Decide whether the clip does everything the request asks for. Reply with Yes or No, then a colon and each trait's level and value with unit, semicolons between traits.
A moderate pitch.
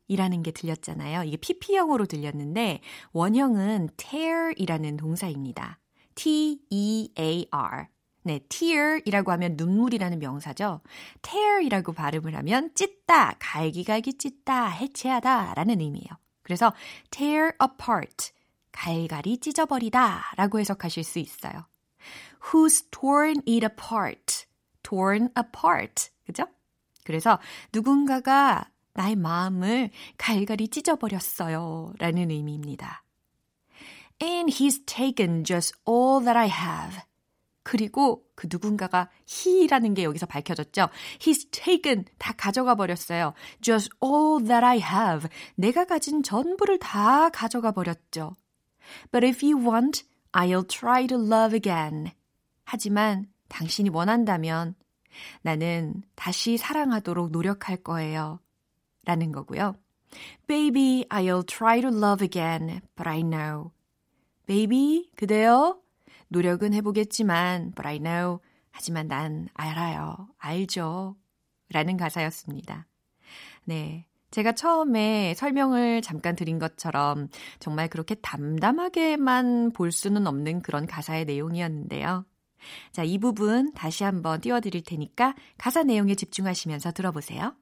No: high, 200 Hz